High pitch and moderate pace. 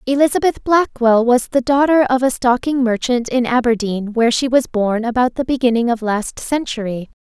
Yes: high, 245 Hz; average, 175 wpm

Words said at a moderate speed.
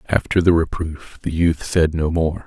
Yes: average, 195 wpm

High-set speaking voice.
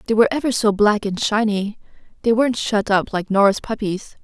Yes: high, 210 Hz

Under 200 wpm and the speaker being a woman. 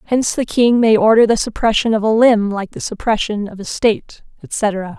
No: fast, 205 wpm; female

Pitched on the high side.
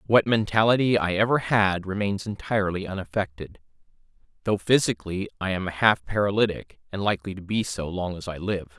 No: low, 100 Hz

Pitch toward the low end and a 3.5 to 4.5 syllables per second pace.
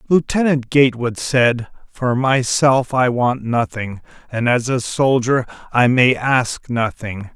Yes: low, 125 Hz; 3.7 syllables/s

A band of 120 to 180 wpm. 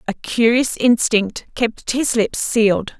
Yes: average, 140 wpm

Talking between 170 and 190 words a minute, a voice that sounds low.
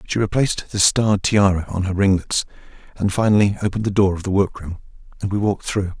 No: average, 200 wpm; low, 100 Hz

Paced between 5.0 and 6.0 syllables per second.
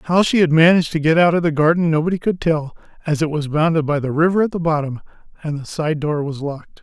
No: 6.4 syllables/s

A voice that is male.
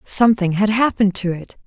No: female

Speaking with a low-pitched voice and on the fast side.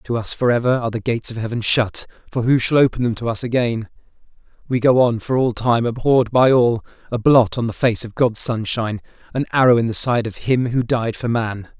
Yes: low, 120 Hz; fast, 235 wpm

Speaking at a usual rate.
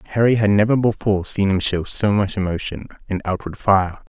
Yes: average, 190 wpm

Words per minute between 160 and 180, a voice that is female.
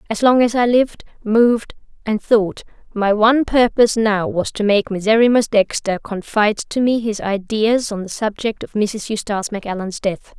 Yes: average, 175 wpm; female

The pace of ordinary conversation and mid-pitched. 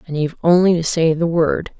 No: fast, 235 wpm; medium, 165 Hz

